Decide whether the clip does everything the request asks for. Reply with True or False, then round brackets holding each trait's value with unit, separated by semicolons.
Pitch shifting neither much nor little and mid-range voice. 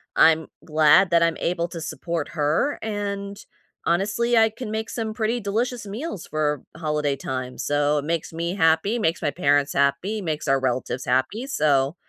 False (5.9 semitones; 165 Hz)